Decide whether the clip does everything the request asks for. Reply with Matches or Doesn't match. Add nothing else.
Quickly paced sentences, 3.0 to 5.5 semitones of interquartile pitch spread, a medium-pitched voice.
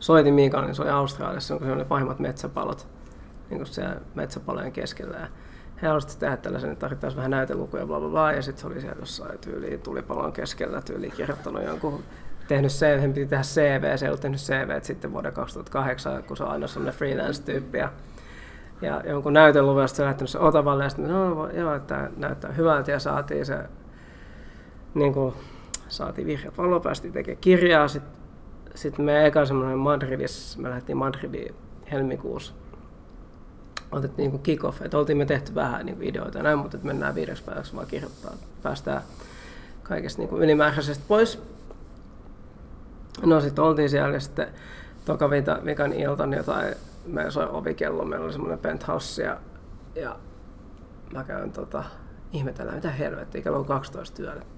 Doesn't match